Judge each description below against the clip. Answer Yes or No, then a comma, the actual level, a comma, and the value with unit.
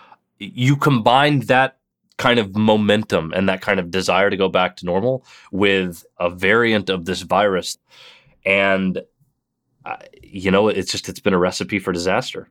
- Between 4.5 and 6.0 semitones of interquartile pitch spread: Yes, average, 5.2 semitones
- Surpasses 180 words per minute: No, average, 160 wpm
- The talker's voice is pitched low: Yes, low, 105 Hz